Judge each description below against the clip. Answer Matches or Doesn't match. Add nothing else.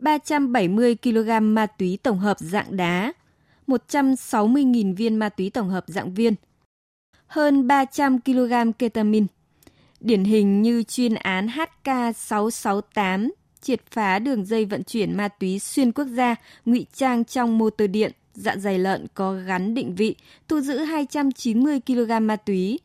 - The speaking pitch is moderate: Doesn't match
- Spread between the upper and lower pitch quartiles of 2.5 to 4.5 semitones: Matches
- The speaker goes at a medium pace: Doesn't match